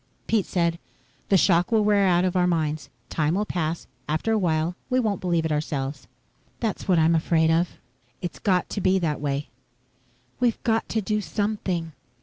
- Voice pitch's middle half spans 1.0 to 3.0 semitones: No, average, 4.1 semitones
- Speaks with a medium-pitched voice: Yes, medium, 175 Hz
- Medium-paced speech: Yes, average, 180 wpm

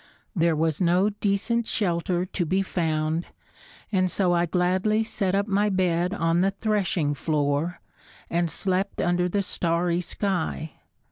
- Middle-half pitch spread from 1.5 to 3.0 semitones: Yes, average, 2.7 semitones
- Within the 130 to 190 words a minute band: Yes, average, 140 wpm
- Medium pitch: Yes, medium, 180 Hz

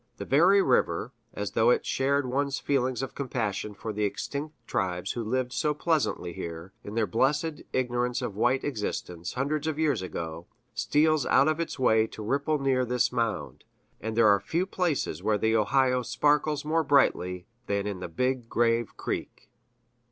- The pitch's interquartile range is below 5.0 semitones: No, average, 5.3 semitones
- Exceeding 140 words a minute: Yes, average, 175 wpm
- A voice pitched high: No, low, 125 Hz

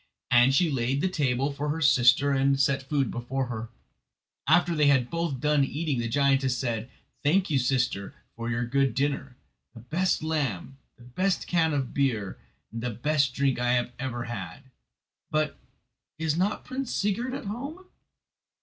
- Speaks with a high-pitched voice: No, low, 135 Hz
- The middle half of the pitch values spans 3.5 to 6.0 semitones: Yes, average, 4.0 semitones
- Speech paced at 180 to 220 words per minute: No, average, 160 wpm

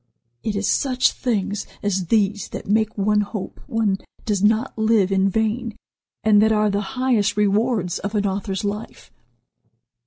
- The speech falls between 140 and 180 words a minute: Yes, average, 155 wpm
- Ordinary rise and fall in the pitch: No, narrow, 1.7 semitones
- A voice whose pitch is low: No, high, 210 Hz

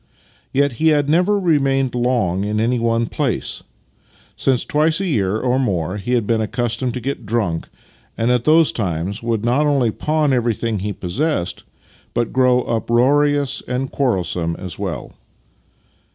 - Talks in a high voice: No, low, 120 Hz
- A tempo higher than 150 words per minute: Yes, average, 160 wpm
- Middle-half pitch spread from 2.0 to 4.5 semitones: No, average, 4.9 semitones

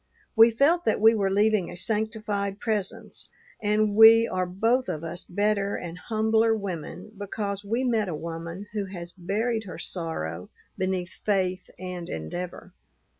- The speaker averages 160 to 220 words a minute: No, average, 150 wpm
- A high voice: Yes, high, 200 Hz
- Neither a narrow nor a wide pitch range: Yes, average, 3.4 semitones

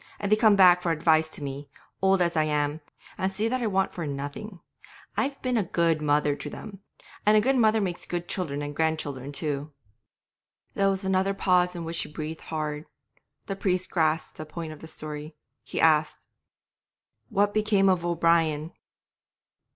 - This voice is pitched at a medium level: Yes, medium, 170 Hz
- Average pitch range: Yes, average, 4.1 semitones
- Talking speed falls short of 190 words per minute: Yes, average, 180 wpm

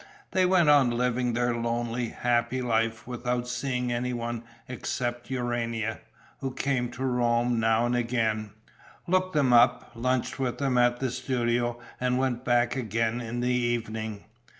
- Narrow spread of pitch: Yes, narrow, 1.2 semitones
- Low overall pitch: Yes, low, 120 Hz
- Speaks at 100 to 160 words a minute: Yes, average, 150 wpm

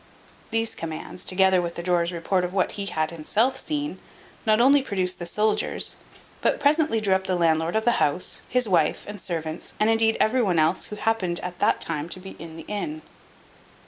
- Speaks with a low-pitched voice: No, high, 190 Hz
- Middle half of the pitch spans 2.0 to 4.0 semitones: No, average, 4.6 semitones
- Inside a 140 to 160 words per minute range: No, average, 200 wpm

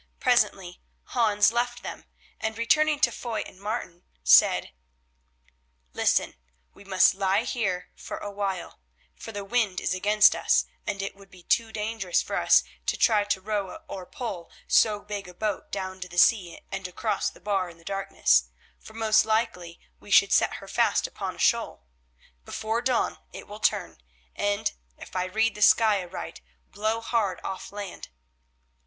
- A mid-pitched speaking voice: No, high, 205 Hz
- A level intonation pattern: No, average, 3.0 semitones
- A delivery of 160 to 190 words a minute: Yes, average, 165 wpm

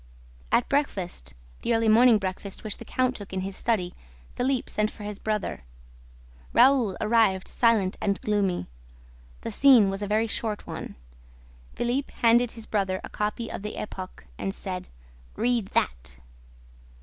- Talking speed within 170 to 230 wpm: No, average, 150 wpm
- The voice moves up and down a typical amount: Yes, average, 3.4 semitones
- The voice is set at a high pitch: Yes, high, 210 Hz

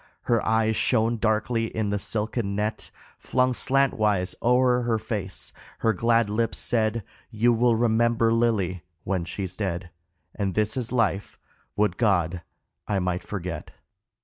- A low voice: Yes, low, 110 Hz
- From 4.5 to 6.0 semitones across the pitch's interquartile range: No, average, 2.9 semitones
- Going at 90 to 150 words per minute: Yes, average, 140 wpm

